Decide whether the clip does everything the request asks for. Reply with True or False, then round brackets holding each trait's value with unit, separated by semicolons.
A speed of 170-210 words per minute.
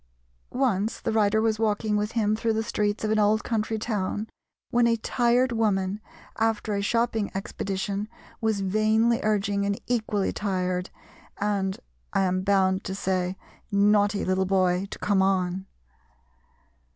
False (145 wpm)